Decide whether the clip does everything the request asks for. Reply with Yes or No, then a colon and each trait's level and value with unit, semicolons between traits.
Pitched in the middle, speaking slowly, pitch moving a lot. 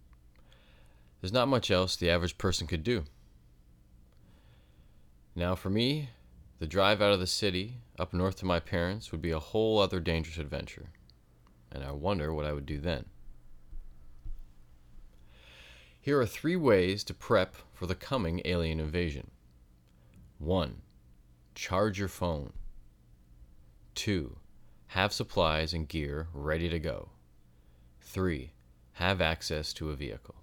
No: very low, 75 Hz; slow, 130 wpm; wide, 6.8 semitones